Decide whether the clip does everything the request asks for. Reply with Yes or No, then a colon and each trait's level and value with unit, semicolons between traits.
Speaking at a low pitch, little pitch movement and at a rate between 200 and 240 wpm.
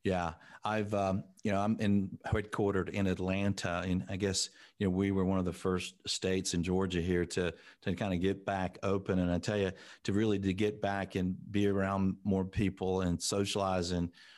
Yes: very low, 95 Hz; narrow, 1.4 semitones; fast, 205 wpm